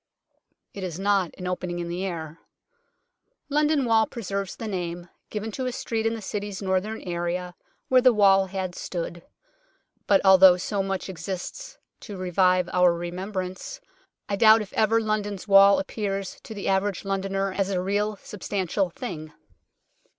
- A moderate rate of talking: Yes, average, 155 wpm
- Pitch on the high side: Yes, high, 195 Hz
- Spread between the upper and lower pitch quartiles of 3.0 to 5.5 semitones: No, narrow, 2.4 semitones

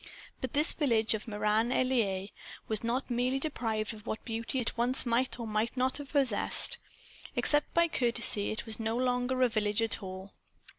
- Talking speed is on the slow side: No, average, 185 wpm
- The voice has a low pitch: No, high, 235 Hz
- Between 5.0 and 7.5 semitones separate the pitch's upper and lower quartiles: No, average, 2.9 semitones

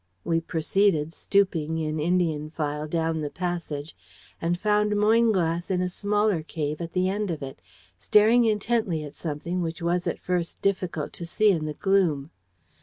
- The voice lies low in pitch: No, medium, 170 Hz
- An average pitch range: Yes, average, 4.1 semitones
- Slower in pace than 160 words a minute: No, average, 165 wpm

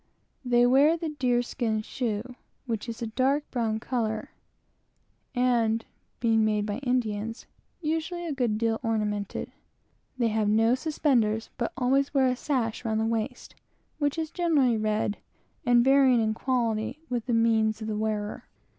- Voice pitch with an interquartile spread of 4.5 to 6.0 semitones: No, average, 3.0 semitones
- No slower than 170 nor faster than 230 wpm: No, average, 155 wpm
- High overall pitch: Yes, high, 235 Hz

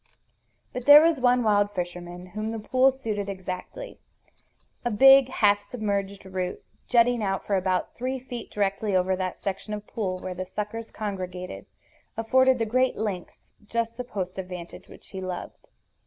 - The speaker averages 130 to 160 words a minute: No, average, 170 wpm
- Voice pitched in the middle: No, high, 205 Hz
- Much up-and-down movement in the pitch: No, average, 4.4 semitones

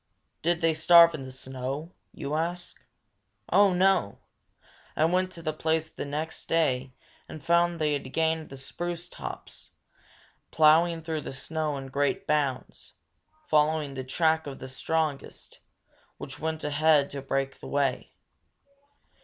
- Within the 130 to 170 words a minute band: Yes, average, 145 wpm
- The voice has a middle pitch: Yes, medium, 155 Hz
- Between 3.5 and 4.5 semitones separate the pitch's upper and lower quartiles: No, average, 3.0 semitones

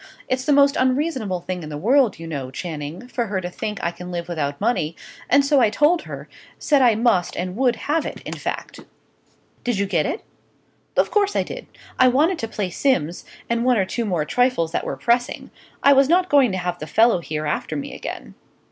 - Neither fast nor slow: No, fast, 220 wpm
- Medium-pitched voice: No, high, 220 Hz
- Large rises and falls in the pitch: Yes, wide, 7.2 semitones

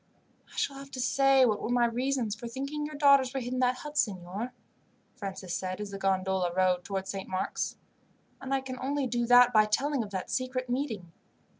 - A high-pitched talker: Yes, high, 245 Hz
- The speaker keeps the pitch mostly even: No, wide, 5.4 semitones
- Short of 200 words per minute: No, fast, 205 wpm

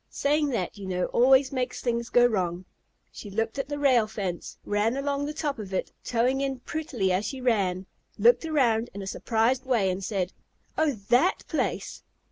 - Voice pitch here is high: Yes, high, 235 Hz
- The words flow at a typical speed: Yes, average, 185 wpm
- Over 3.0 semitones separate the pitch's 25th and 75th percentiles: Yes, average, 5.3 semitones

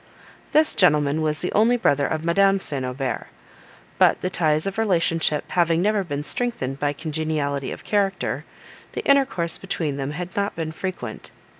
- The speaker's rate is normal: Yes, average, 160 wpm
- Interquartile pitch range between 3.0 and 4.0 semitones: No, average, 4.8 semitones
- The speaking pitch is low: No, medium, 165 Hz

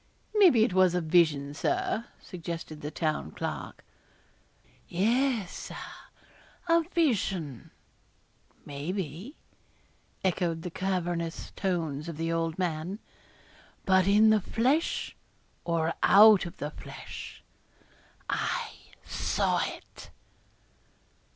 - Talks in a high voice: No, medium, 180 Hz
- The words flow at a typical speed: No, slow, 100 wpm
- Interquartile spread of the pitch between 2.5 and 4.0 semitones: No, average, 4.6 semitones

